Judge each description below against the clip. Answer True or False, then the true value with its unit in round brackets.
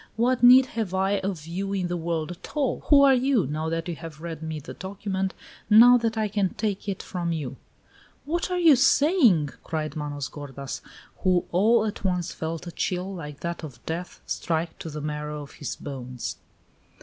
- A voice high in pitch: False (180 Hz)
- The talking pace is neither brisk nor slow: True (195 wpm)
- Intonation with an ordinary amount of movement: False (5.7 semitones)